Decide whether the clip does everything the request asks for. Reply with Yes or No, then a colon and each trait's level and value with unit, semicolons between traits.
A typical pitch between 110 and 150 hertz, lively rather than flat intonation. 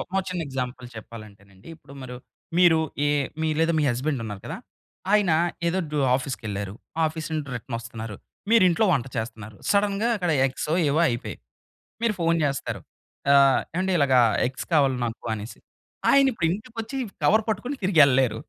Yes: medium, 140 Hz; wide, 7.3 semitones